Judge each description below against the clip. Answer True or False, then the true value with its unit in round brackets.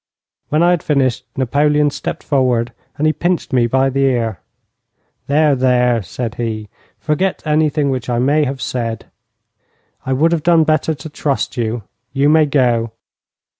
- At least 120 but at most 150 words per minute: False (160 wpm)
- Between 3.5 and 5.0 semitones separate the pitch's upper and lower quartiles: True (3.9 semitones)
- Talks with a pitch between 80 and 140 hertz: True (135 Hz)